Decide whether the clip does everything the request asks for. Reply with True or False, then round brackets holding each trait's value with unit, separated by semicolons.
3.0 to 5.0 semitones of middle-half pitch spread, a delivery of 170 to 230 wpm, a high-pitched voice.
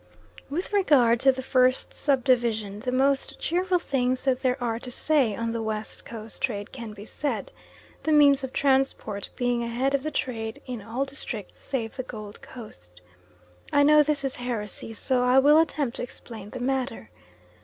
True (3.4 semitones; 180 wpm; 250 Hz)